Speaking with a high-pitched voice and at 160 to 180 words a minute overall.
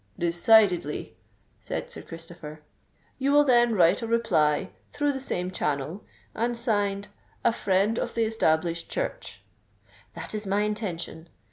No: high, 200 Hz; slow, 135 wpm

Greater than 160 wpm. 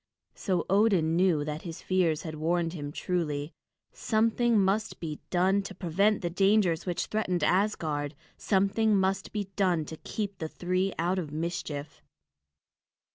No: average, 145 wpm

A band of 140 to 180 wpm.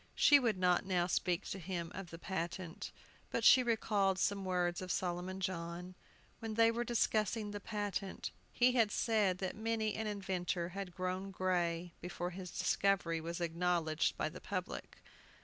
Yes: average, 165 wpm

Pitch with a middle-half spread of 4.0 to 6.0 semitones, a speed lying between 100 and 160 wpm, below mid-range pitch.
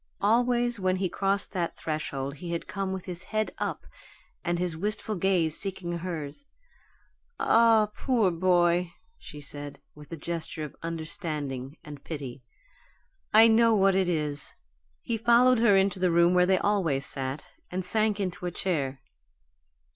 No: average, 4.5 semitones; average, 155 wpm; medium, 180 Hz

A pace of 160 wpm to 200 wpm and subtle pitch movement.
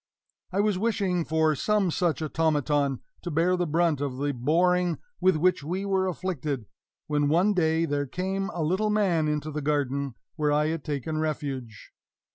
No: average, 170 wpm; average, 3.8 semitones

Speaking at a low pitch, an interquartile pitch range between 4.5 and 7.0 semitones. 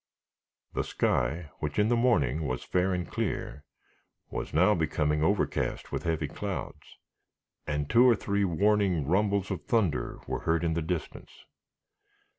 Yes: very low, 85 Hz; average, 5.1 semitones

